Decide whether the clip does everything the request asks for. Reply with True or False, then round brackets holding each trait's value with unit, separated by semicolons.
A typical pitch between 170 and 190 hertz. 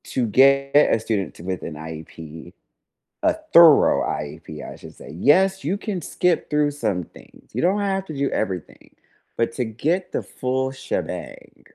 False (130 Hz)